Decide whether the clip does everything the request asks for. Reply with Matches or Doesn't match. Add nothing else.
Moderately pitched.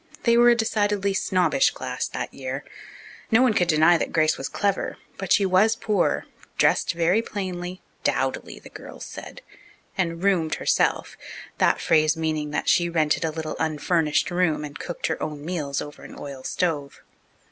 Matches